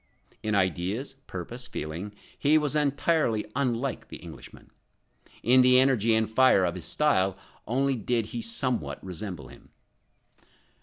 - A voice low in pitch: Yes, low, 115 Hz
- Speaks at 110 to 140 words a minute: Yes, slow, 135 wpm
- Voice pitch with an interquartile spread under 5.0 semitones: No, wide, 5.6 semitones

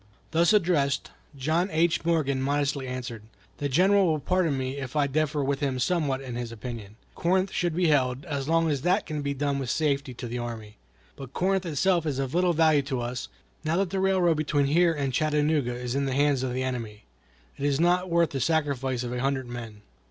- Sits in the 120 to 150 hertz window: Yes, medium, 140 Hz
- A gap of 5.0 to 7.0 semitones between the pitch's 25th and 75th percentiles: No, average, 4.2 semitones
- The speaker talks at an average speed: No, fast, 210 wpm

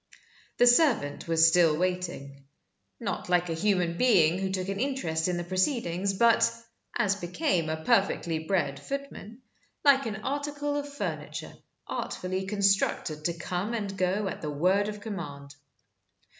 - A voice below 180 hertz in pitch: No, high, 190 Hz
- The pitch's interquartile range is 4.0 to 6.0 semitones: Yes, average, 5.0 semitones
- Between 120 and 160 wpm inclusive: Yes, average, 145 wpm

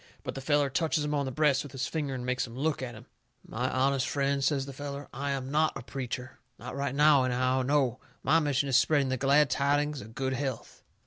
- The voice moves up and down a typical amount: No, narrow, 1.9 semitones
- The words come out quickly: Yes, fast, 235 wpm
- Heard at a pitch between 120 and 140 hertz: Yes, low, 135 Hz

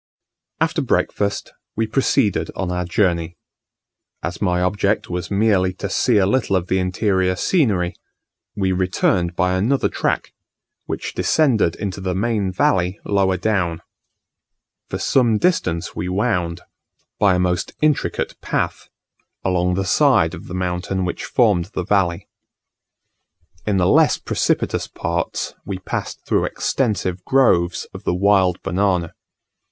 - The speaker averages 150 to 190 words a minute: No, slow, 135 wpm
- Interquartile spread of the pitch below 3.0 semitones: Yes, narrow, 2.5 semitones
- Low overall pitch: Yes, very low, 95 Hz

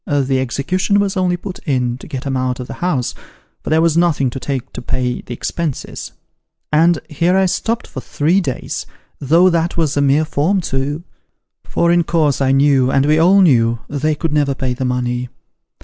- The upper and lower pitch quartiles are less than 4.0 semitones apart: No, average, 4.6 semitones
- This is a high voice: No, medium, 145 Hz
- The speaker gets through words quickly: No, average, 195 wpm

